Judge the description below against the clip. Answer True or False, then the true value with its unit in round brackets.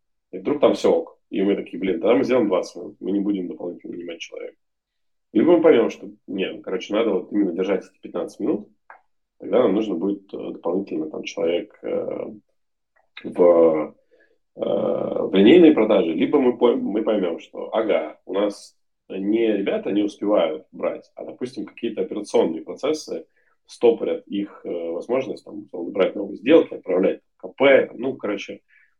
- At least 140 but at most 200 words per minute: True (155 wpm)